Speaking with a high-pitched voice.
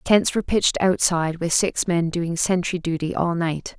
No: medium, 175 Hz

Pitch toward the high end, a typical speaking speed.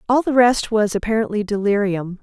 Yes: high, 215 Hz; average, 160 wpm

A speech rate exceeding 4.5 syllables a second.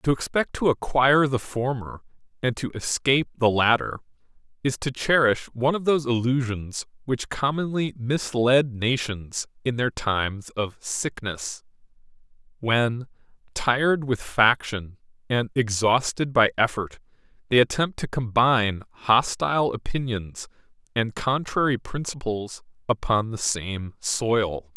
No: 4.2 syllables/s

